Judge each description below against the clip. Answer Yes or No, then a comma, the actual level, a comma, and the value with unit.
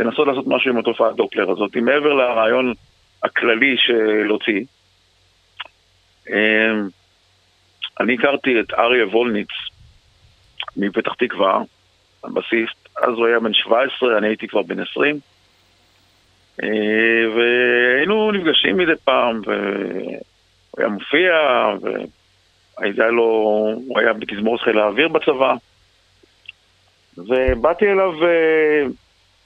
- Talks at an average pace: No, slow, 95 wpm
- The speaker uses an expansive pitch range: No, average, 4.4 semitones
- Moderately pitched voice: No, low, 110 Hz